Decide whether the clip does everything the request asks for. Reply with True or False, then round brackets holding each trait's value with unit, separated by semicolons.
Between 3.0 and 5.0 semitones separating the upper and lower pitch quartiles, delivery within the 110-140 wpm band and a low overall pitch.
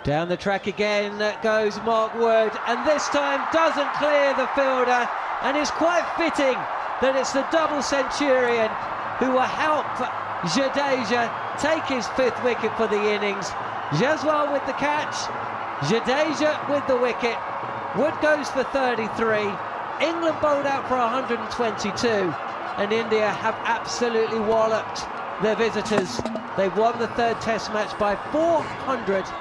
False (4.5 semitones; 135 wpm; 235 Hz)